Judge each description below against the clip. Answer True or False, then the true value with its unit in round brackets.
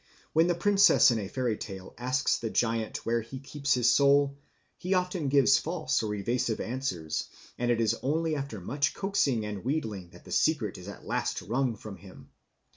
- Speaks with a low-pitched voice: True (125 Hz)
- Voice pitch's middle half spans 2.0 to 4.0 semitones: False (4.9 semitones)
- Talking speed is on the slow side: False (190 wpm)